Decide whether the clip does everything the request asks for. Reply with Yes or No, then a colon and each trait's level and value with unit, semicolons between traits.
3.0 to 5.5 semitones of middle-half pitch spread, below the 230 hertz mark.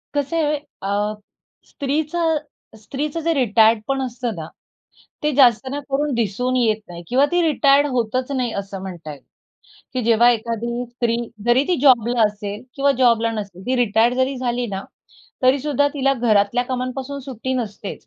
No: average, 3.7 semitones; high, 245 Hz